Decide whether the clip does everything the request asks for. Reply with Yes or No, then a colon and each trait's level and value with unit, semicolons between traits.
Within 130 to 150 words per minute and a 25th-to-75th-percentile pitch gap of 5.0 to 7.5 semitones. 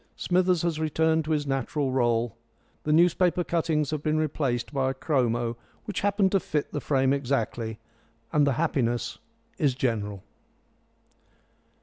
No: average, 140 wpm; average, 4.5 semitones